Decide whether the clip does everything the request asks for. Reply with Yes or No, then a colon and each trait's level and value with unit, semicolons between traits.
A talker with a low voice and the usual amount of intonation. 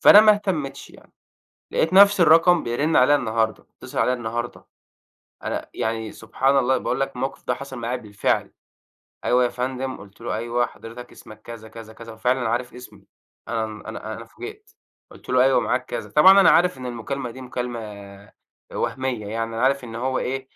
Yes: low, 125 Hz; average, 3.1 semitones